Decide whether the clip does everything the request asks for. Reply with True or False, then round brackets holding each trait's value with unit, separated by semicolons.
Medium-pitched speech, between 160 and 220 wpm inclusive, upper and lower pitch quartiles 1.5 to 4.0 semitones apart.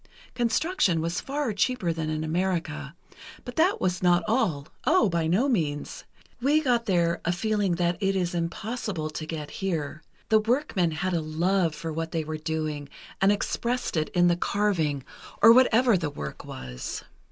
False (175 Hz; 165 wpm; 5.6 semitones)